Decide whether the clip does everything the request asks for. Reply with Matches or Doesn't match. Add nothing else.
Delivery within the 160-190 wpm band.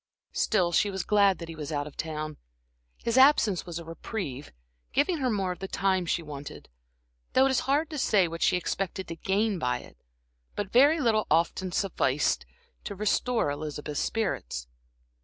Matches